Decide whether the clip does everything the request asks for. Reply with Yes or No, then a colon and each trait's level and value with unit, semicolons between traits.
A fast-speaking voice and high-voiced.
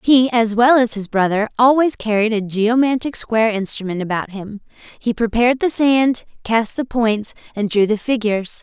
No: average, 175 wpm; high, 230 Hz